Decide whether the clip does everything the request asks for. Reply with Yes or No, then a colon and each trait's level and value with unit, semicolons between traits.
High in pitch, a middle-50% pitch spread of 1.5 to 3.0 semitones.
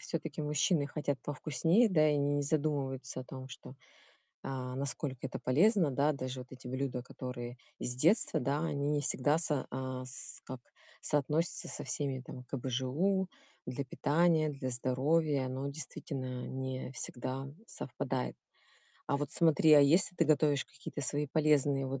No: medium, 140 Hz; average, 2.7 semitones